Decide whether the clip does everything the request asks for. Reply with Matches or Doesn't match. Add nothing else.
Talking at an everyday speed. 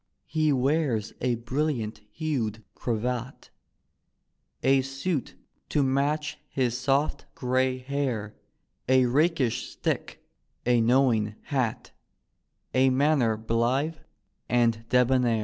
Doesn't match